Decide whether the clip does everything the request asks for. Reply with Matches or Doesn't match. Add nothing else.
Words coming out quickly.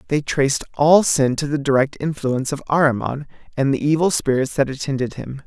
Doesn't match